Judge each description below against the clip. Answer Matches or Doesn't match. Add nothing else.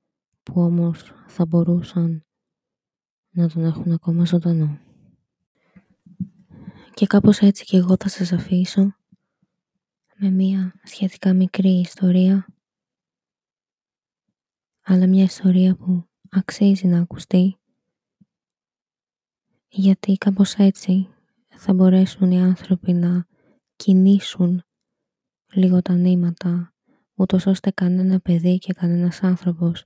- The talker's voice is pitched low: Doesn't match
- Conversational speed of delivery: Doesn't match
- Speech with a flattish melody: Matches